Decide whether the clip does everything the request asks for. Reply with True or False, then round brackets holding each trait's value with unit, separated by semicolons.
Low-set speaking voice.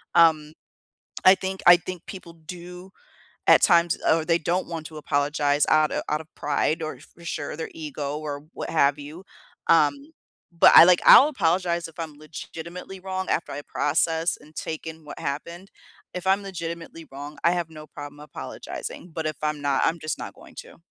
False (160 Hz)